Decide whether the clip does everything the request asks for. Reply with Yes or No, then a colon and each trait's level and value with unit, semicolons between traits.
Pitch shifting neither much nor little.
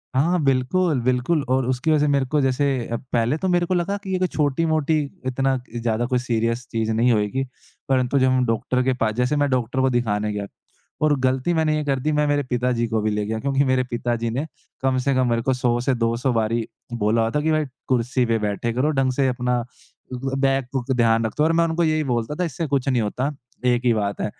Yes: average, 3.5 semitones